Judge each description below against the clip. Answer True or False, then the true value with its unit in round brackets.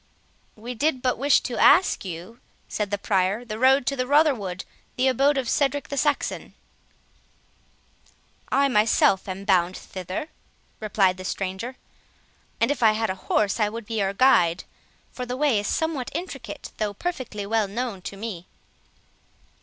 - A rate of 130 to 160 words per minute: True (155 wpm)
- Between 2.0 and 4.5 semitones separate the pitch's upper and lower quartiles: False (5.1 semitones)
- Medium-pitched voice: False (225 Hz)